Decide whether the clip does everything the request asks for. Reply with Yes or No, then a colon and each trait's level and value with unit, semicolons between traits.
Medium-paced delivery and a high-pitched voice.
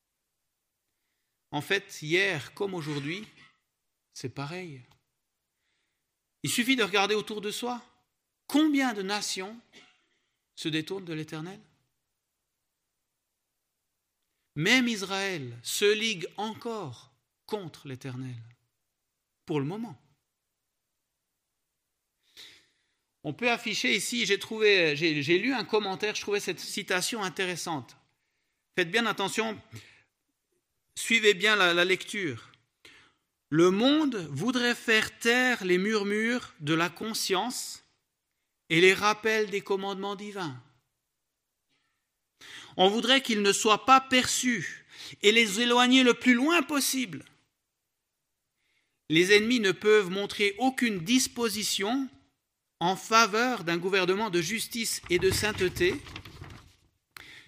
No: slow, 105 wpm; high, 200 Hz